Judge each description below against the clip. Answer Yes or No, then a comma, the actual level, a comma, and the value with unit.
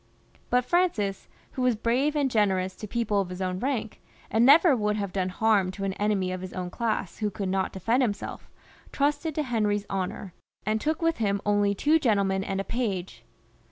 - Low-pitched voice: No, high, 210 Hz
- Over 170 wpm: Yes, average, 195 wpm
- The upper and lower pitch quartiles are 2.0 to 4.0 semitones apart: No, average, 4.4 semitones